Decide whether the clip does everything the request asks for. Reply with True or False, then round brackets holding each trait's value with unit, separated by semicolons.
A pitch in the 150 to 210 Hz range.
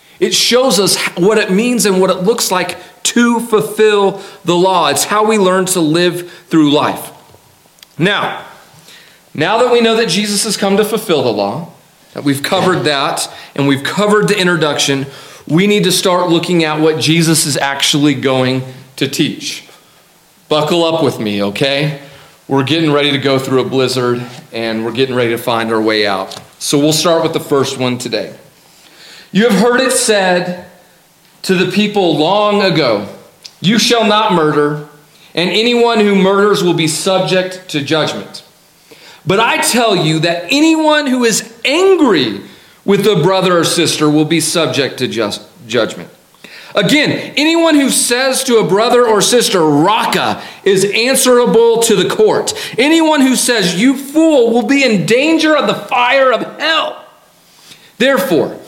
True (185 Hz)